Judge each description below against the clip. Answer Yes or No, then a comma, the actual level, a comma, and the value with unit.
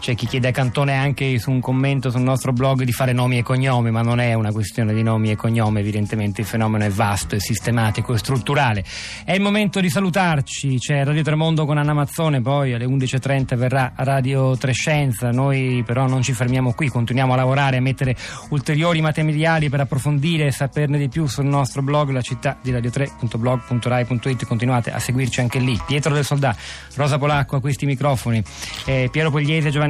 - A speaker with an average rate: No, fast, 190 wpm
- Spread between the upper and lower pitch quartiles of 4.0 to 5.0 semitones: No, average, 2.9 semitones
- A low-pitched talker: Yes, low, 130 Hz